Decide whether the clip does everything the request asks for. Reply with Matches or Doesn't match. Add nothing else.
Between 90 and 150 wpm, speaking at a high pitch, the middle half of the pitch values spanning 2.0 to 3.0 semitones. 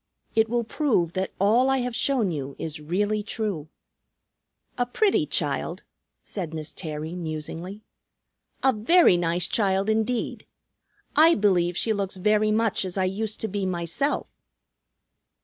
Doesn't match